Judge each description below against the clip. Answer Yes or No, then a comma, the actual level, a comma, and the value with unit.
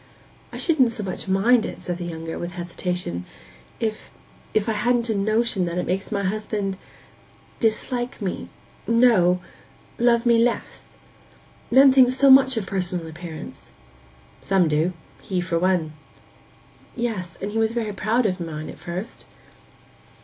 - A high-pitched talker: Yes, high, 200 Hz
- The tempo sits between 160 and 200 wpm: No, slow, 135 wpm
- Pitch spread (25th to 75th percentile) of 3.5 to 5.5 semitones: Yes, average, 4.7 semitones